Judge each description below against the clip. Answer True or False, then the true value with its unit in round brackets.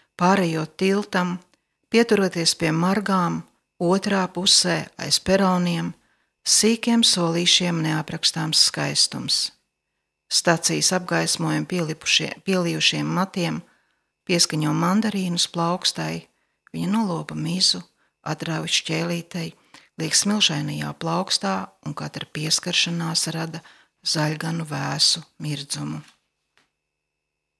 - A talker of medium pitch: True (165 Hz)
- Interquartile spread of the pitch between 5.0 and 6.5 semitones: False (3.2 semitones)